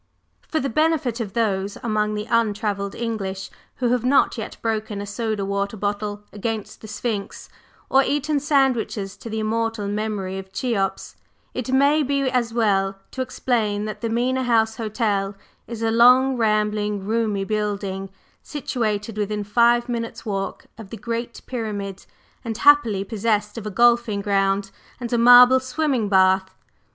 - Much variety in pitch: No, average, 2.9 semitones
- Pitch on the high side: Yes, high, 220 Hz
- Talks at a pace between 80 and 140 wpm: No, average, 155 wpm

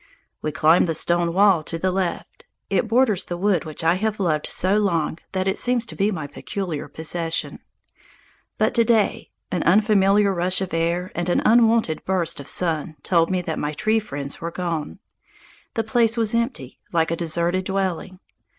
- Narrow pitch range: No, average, 3.8 semitones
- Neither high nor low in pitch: Yes, medium, 180 Hz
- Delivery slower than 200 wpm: Yes, average, 180 wpm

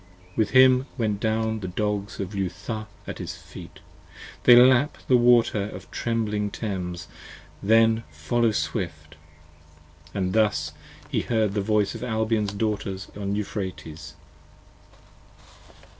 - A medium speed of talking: No, slow, 125 wpm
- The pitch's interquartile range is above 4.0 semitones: No, narrow, 2.5 semitones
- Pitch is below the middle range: Yes, low, 105 Hz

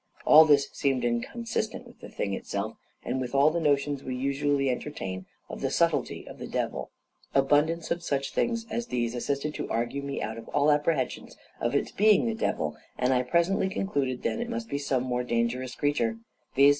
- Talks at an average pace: Yes, average, 195 wpm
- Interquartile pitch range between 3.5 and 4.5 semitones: Yes, average, 4.2 semitones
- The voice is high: No, medium, 140 Hz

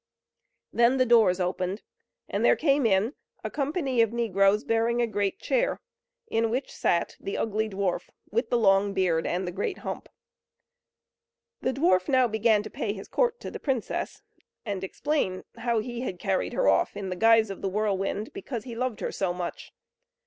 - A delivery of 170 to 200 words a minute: Yes, average, 180 wpm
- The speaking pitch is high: Yes, high, 220 Hz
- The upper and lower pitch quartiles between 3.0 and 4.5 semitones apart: Yes, average, 4.1 semitones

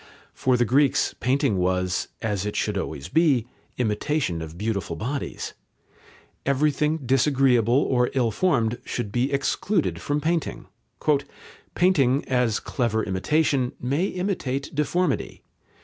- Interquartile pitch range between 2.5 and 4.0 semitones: No, average, 5.0 semitones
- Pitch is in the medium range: No, low, 130 Hz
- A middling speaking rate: No, slow, 115 wpm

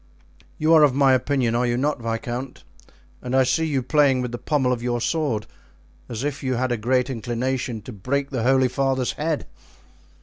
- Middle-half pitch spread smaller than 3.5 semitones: Yes, narrow, 2.5 semitones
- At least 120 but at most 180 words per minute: No, average, 195 wpm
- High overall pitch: No, low, 130 Hz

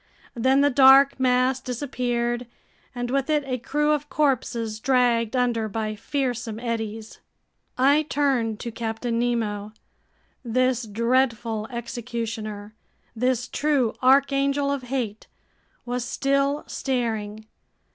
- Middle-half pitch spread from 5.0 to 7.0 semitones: No, average, 3.0 semitones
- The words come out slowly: Yes, slow, 110 wpm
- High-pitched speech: Yes, high, 245 Hz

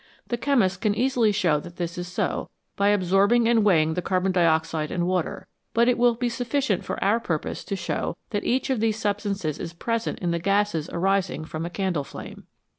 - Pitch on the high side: Yes, high, 195 Hz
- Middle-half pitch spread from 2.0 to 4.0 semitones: No, average, 4.8 semitones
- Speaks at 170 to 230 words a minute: Yes, average, 200 wpm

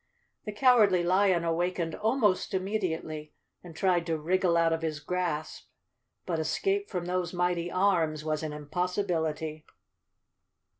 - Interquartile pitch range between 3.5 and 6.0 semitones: No, average, 2.7 semitones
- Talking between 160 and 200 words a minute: No, slow, 135 wpm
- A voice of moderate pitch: Yes, medium, 175 Hz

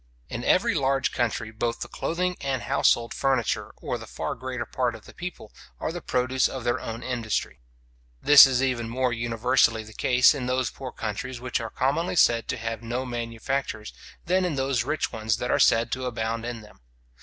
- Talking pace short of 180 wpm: No, average, 195 wpm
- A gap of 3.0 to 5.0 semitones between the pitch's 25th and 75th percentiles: No, narrow, 2.5 semitones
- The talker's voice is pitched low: Yes, low, 125 Hz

